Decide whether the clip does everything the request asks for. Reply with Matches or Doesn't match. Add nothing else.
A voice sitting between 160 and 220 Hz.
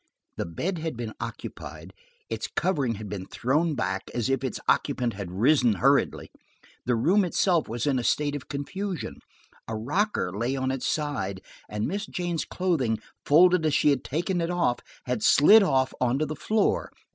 Doesn't match